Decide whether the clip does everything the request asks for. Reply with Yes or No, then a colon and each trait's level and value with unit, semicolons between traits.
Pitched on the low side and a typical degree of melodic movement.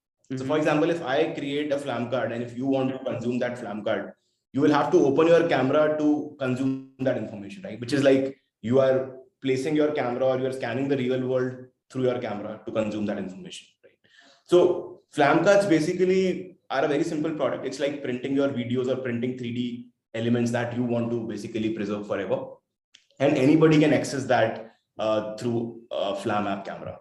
Yes: low, 130 Hz; average, 3.5 semitones